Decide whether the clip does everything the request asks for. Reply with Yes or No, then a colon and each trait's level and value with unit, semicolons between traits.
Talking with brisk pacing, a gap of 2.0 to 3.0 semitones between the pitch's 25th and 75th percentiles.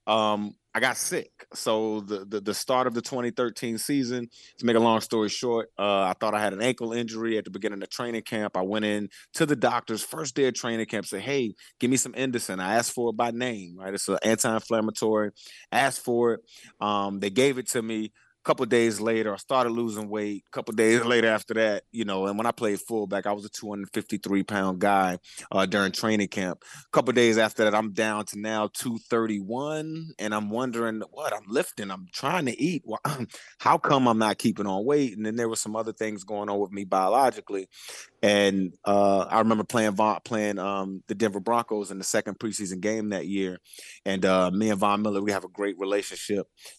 Yes: fast, 220 wpm; narrow, 2.5 semitones